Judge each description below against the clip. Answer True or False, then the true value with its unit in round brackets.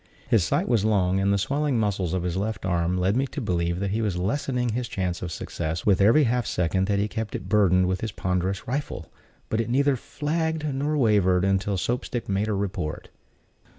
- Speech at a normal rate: False (215 wpm)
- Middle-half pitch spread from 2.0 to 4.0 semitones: False (4.6 semitones)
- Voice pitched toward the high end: False (100 Hz)